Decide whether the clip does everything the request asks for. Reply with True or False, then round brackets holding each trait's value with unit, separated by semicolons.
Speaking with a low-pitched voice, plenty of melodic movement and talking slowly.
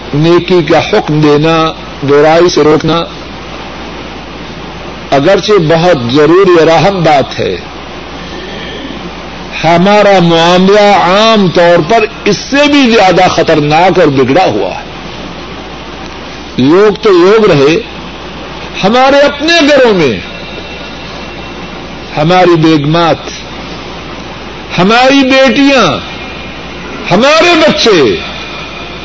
False (180 Hz; 7.6 semitones; 85 wpm)